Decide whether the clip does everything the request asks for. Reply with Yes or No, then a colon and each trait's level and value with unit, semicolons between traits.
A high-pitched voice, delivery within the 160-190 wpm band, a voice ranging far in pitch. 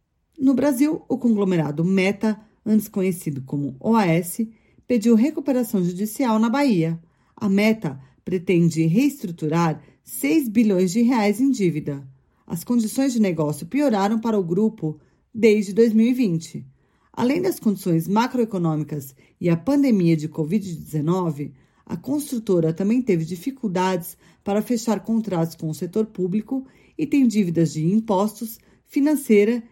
No: high, 205 Hz; average, 125 wpm; wide, 5.9 semitones